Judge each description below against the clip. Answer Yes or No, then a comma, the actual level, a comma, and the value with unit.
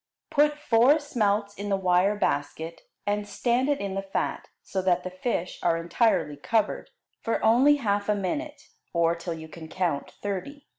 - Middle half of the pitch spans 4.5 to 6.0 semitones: Yes, average, 5.2 semitones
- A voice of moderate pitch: No, high, 200 Hz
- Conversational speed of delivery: Yes, average, 170 wpm